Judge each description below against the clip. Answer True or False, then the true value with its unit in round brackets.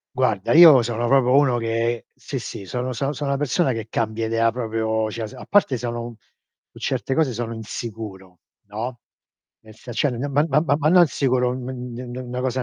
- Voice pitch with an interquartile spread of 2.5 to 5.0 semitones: True (2.8 semitones)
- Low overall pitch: True (120 Hz)